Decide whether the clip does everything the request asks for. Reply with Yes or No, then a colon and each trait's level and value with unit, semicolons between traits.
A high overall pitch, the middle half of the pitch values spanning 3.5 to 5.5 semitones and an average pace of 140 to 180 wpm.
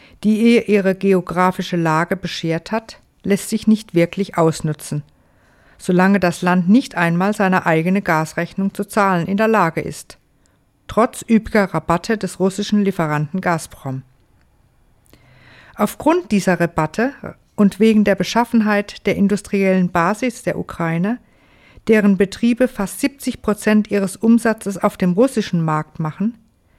No: high, 195 Hz; average, 4.0 semitones; average, 130 wpm